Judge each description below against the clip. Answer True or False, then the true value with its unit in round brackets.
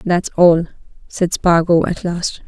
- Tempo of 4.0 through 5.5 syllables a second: False (3.6 syllables/s)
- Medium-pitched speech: True (175 Hz)